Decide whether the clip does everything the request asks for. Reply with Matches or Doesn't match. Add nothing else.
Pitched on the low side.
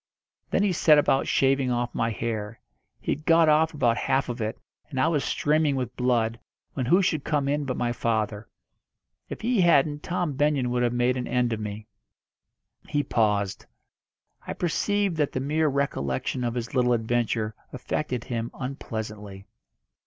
Matches